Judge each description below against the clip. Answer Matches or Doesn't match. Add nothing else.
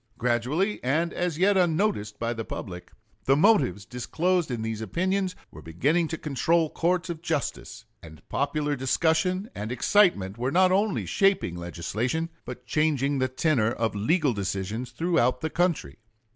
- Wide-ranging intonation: Matches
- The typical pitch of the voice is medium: Matches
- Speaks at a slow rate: Doesn't match